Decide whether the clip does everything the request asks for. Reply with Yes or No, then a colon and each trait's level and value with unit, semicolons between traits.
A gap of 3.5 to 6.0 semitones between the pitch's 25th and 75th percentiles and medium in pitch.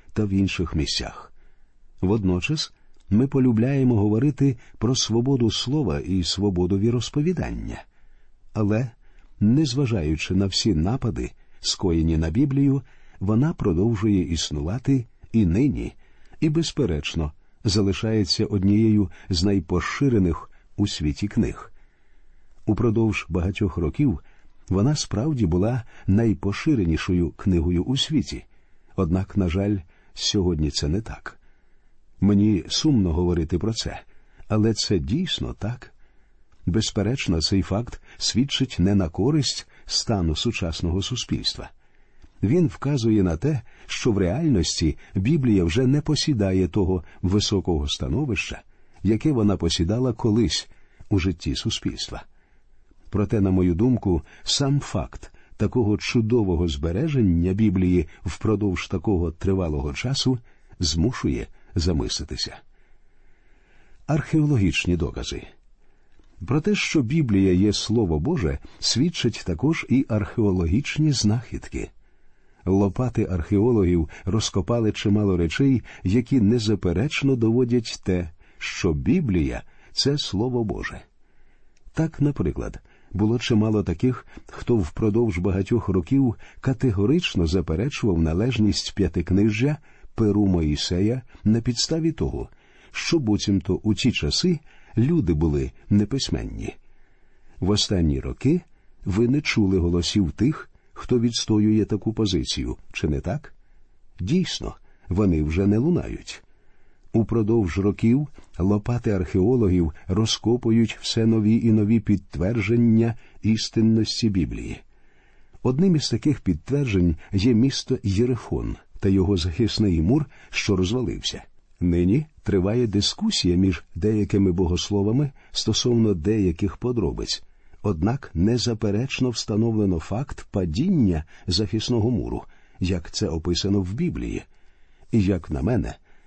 No: average, 4.8 semitones; low, 105 Hz